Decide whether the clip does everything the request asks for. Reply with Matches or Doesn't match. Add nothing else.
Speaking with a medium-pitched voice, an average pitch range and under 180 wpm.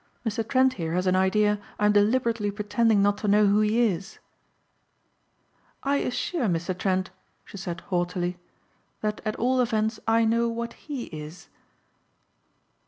Doesn't match